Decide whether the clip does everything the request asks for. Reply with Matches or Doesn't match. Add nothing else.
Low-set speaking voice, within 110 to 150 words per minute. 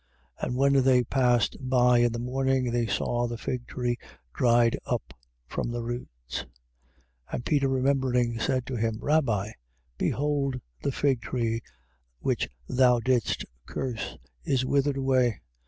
Matches